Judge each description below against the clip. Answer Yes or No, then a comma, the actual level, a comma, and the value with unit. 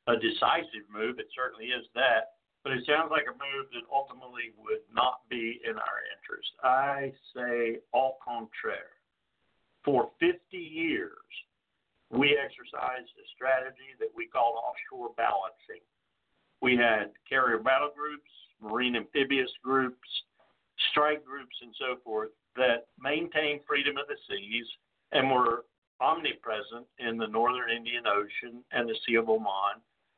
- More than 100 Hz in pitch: Yes, low, 135 Hz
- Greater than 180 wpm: No, slow, 135 wpm